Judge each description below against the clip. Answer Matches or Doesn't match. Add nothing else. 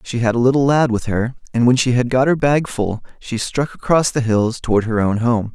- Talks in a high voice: Doesn't match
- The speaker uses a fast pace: Matches